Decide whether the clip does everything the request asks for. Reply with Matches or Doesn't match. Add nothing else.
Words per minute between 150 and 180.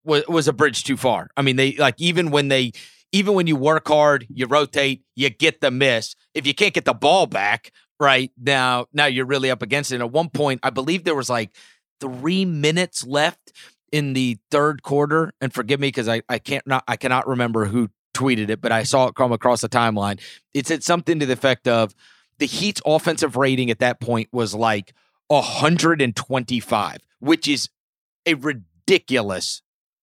Doesn't match